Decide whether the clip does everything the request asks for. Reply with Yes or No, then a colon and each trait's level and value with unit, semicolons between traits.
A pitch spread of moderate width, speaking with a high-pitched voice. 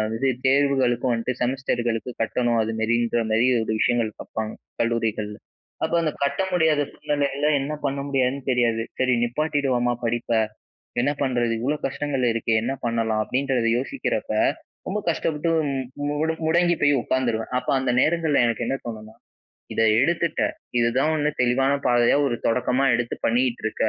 No: average, 3.3 semitones; low, 125 Hz